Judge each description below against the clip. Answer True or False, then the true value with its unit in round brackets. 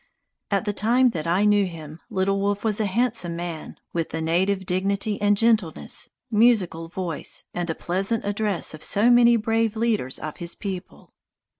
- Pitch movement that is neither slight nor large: True (4.1 semitones)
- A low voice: False (200 Hz)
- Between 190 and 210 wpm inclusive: False (165 wpm)